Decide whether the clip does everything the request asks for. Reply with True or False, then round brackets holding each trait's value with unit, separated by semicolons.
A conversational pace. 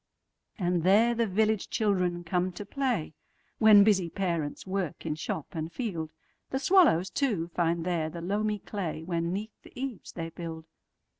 True (145 wpm)